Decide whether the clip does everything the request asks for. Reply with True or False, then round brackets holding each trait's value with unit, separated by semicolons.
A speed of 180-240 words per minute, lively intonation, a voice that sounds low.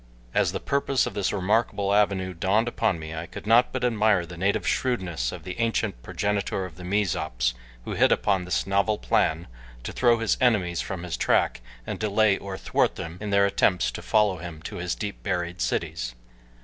False (195 wpm; 3.5 semitones; 95 Hz)